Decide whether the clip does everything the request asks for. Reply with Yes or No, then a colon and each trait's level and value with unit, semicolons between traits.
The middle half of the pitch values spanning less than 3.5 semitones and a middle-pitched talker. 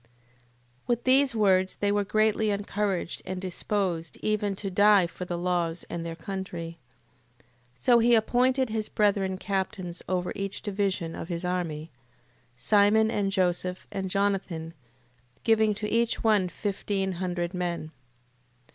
No: average, 2.9 semitones; high, 195 Hz